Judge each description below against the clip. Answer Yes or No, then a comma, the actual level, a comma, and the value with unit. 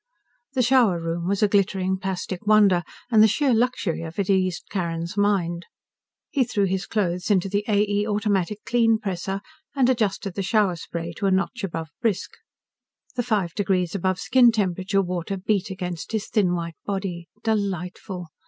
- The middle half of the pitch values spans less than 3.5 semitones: Yes, average, 3.0 semitones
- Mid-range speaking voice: No, high, 195 Hz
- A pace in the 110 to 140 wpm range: No, average, 170 wpm